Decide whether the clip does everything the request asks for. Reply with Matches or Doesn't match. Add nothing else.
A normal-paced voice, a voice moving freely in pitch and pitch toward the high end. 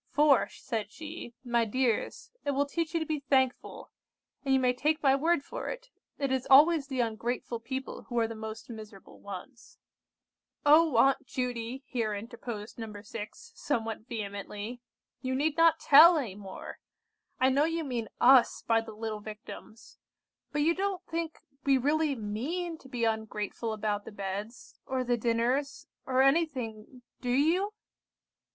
Doesn't match